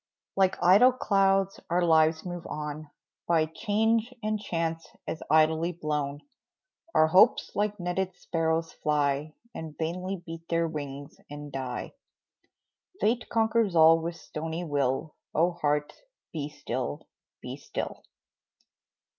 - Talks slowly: Yes, slow, 120 wpm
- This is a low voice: No, medium, 165 Hz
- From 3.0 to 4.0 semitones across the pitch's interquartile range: Yes, average, 3.4 semitones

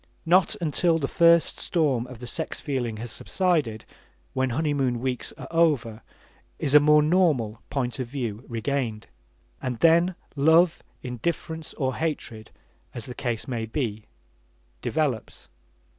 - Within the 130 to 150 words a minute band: Yes, slow, 135 wpm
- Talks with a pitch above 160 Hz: No, low, 135 Hz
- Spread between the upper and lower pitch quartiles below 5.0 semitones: No, average, 5.3 semitones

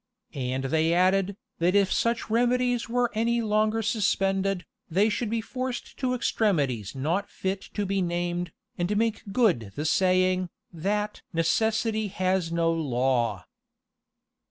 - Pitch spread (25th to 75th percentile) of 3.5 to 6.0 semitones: Yes, average, 4.8 semitones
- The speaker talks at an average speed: No, slow, 130 wpm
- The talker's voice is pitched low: No, high, 195 Hz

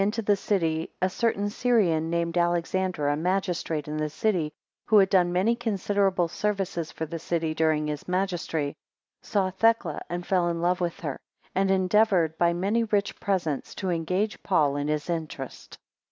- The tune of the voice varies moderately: Yes, average, 3.5 semitones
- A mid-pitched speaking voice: Yes, medium, 175 Hz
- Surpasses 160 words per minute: Yes, average, 170 wpm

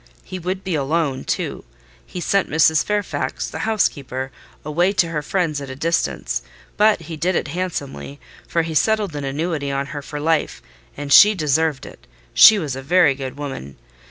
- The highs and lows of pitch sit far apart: No, average, 4.5 semitones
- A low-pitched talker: No, medium, 155 Hz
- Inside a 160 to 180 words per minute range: Yes, average, 175 wpm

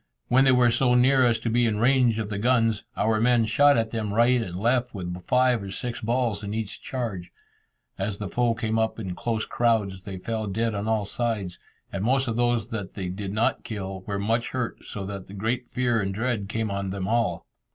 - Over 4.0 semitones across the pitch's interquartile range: No, average, 3.2 semitones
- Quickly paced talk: Yes, fast, 220 wpm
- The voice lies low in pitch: Yes, low, 110 Hz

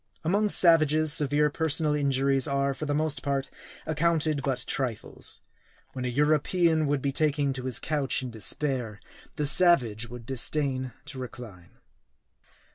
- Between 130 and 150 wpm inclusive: Yes, average, 140 wpm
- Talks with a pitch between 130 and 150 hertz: Yes, medium, 140 Hz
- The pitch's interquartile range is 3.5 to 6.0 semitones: No, average, 2.9 semitones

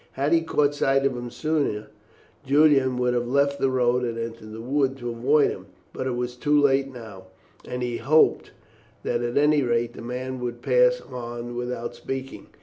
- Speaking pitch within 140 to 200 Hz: No, low, 125 Hz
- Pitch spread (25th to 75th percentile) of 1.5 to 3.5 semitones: Yes, average, 2.7 semitones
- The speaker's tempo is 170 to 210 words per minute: Yes, average, 190 wpm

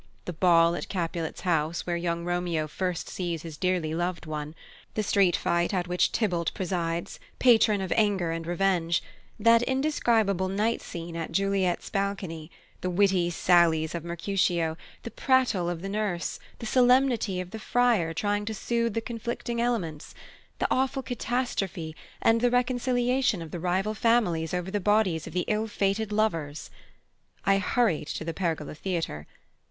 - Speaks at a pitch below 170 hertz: No, medium, 185 Hz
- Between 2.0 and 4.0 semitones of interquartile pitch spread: No, average, 4.5 semitones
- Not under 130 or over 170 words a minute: Yes, average, 160 wpm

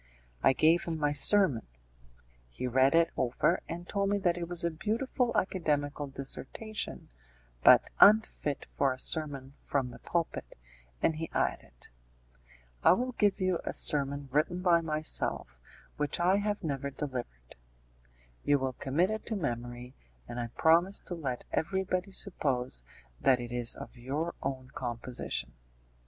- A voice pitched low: No, medium, 150 Hz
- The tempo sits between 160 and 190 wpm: No, average, 145 wpm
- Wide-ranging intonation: Yes, wide, 5.7 semitones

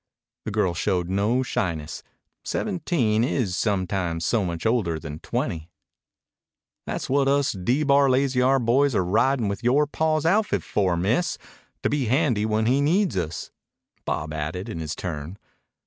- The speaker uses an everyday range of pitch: No, wide, 7.5 semitones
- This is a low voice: Yes, low, 110 Hz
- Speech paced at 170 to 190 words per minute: No, average, 155 wpm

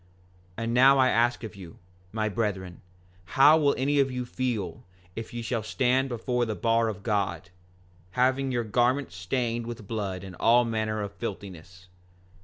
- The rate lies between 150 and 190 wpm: Yes, average, 170 wpm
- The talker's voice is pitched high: No, low, 115 Hz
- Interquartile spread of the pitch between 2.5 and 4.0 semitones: Yes, average, 3.6 semitones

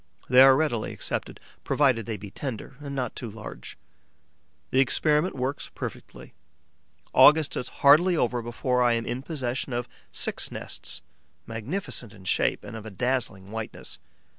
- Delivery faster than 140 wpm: Yes, average, 150 wpm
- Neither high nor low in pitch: No, low, 125 Hz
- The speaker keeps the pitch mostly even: No, average, 3.6 semitones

